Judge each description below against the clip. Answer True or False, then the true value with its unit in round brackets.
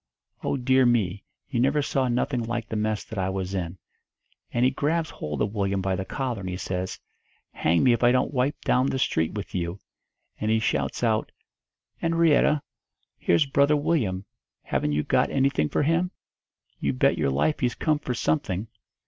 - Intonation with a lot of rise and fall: True (6.3 semitones)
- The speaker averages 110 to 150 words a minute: False (185 wpm)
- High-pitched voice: False (120 Hz)